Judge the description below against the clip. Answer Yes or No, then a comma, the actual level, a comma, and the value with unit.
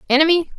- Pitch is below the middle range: No, very high, 310 Hz